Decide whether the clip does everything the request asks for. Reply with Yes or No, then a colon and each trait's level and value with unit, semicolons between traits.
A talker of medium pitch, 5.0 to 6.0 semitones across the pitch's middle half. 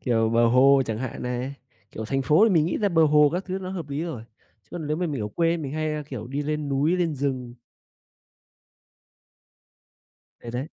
No: medium, 145 Hz; average, 4.3 semitones